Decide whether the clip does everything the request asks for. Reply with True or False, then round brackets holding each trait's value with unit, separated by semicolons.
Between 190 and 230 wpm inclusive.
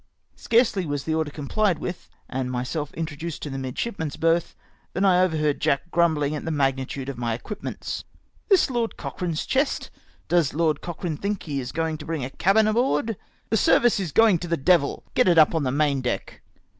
True (200 wpm)